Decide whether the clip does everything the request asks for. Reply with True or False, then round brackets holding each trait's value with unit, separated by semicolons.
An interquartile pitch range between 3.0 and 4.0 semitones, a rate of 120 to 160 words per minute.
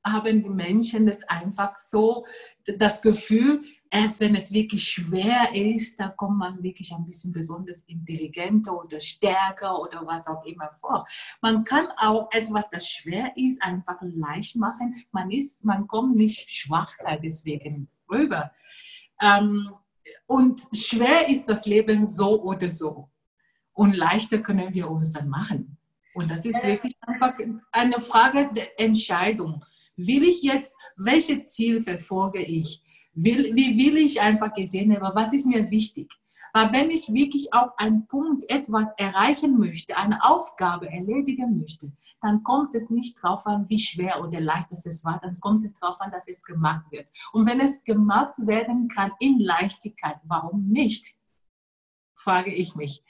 False (4.7 semitones; 155 wpm)